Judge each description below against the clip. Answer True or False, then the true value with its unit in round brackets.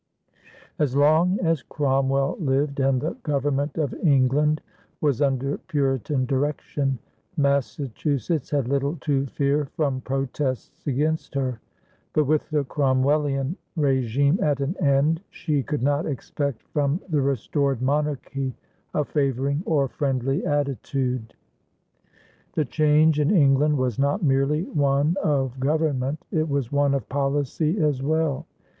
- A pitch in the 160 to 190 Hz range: False (140 Hz)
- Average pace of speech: False (125 wpm)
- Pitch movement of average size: False (1.9 semitones)